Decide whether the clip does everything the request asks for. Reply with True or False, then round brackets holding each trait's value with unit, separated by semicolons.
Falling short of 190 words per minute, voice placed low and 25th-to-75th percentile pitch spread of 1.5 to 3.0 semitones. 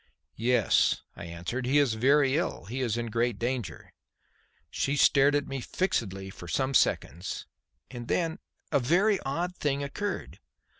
False (155 wpm; 130 Hz; 3.9 semitones)